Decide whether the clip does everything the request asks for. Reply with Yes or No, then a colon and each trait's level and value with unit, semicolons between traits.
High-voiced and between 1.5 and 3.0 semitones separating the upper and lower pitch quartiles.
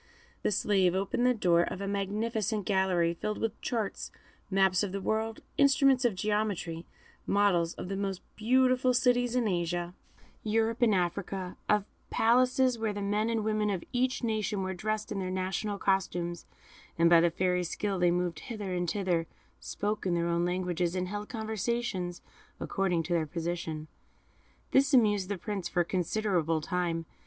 No: high, 195 Hz; average, 3.6 semitones